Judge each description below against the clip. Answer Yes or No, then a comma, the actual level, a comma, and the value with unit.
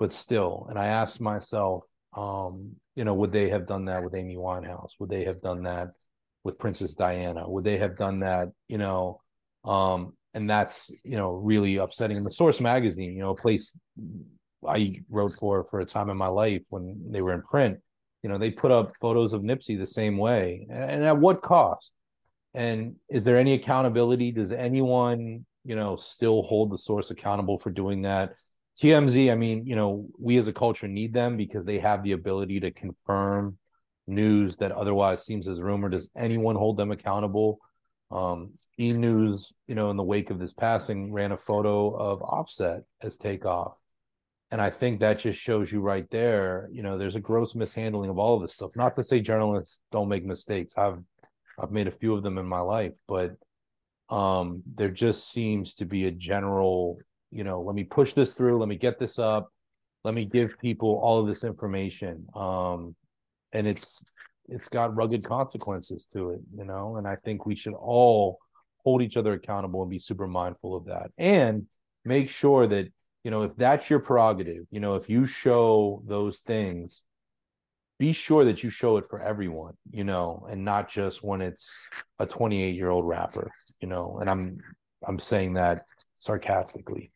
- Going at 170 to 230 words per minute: Yes, average, 190 wpm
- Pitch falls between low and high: No, low, 105 Hz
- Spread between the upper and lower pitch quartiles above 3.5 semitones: No, average, 2.9 semitones